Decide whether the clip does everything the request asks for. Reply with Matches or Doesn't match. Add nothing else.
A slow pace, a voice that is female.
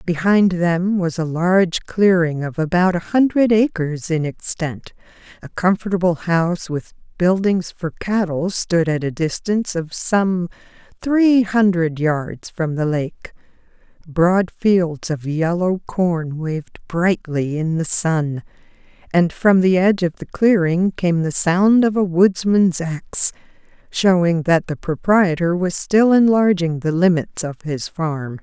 Doesn't match